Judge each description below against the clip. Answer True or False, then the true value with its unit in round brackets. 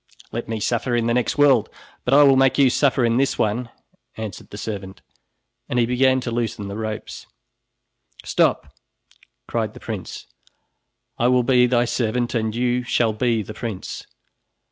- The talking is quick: False (165 wpm)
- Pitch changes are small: True (2.2 semitones)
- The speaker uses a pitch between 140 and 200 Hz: False (120 Hz)